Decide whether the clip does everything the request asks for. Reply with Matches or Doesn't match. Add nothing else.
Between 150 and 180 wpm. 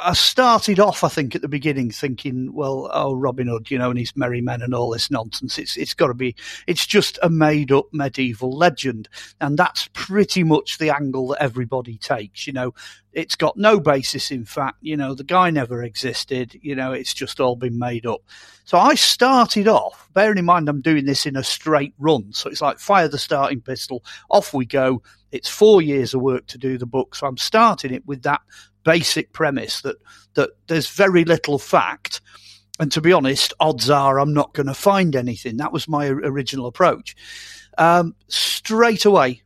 Doesn't match